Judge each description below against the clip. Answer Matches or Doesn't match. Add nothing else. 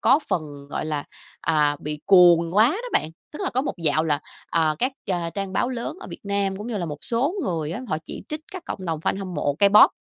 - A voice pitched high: Doesn't match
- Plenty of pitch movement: Matches